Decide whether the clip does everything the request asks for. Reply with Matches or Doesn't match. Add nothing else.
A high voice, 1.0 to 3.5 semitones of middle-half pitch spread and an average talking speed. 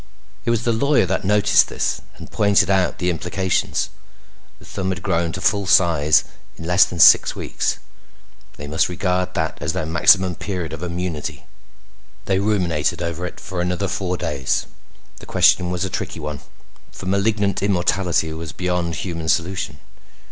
Doesn't match